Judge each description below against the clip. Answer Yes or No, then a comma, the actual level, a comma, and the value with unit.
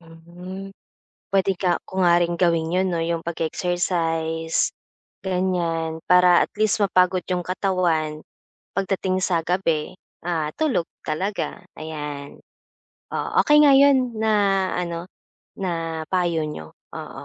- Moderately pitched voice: Yes, medium, 175 Hz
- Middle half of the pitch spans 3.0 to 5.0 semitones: No, narrow, 2.4 semitones